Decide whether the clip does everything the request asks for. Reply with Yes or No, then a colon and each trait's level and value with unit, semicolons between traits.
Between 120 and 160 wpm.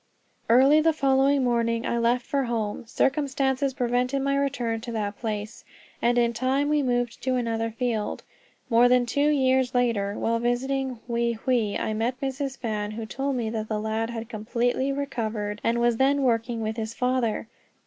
No: average, 175 wpm